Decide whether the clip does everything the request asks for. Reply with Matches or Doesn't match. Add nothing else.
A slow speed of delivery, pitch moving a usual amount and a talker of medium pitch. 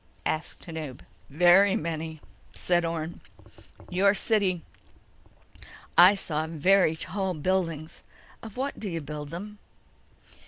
Matches